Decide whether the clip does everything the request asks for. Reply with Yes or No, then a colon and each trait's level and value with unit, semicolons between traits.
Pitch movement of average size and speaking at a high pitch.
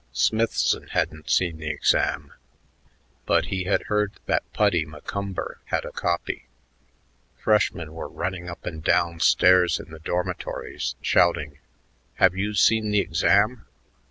No: average, 3.9 semitones; very low, 90 Hz